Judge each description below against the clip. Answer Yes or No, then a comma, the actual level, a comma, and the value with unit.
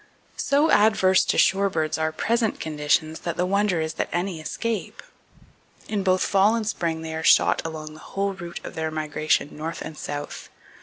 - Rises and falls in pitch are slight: No, average, 4.0 semitones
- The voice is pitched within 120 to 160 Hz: No, medium, 170 Hz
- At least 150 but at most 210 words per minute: Yes, average, 175 wpm